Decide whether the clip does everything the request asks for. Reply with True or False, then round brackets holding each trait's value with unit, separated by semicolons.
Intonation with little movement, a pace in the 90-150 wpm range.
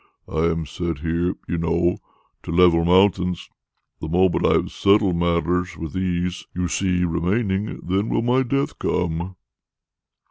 True (2.0 semitones; 145 wpm)